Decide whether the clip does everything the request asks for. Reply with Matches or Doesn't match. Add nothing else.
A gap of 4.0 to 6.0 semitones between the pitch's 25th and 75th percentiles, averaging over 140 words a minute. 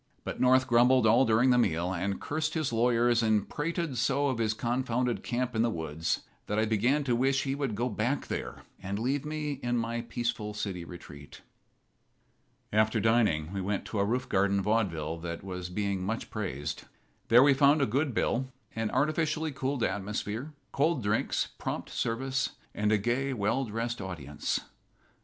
Matches